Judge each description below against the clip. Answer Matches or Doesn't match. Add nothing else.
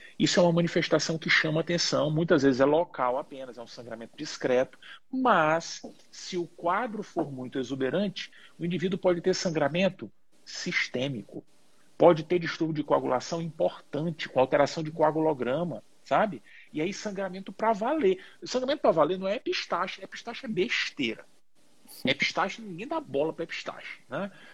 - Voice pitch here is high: Doesn't match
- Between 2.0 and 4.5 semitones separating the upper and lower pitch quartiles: Matches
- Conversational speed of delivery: Matches